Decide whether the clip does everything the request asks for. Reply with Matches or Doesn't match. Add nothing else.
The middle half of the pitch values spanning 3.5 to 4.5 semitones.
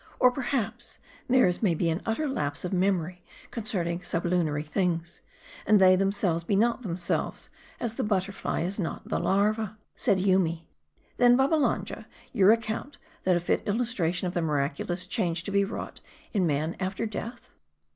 Matches